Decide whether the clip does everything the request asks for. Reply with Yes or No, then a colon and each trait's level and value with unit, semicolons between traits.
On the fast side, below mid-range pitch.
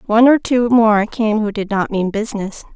No: fast, 220 wpm; high, 220 Hz